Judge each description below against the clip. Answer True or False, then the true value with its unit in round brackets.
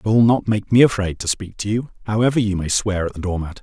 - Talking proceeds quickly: True (280 wpm)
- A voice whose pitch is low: True (105 Hz)